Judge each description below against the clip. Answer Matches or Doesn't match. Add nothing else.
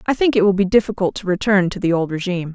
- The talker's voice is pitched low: Doesn't match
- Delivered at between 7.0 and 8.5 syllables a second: Matches